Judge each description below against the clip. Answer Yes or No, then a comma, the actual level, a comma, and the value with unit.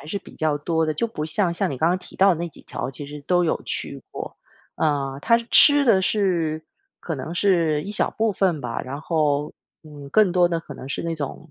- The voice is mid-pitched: Yes, medium, 160 Hz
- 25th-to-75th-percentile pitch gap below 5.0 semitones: Yes, average, 3.8 semitones